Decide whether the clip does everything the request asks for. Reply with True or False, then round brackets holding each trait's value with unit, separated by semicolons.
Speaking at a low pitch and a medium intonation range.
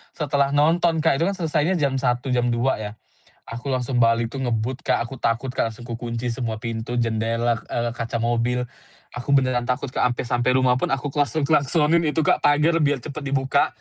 True (125 Hz; 3.5 semitones)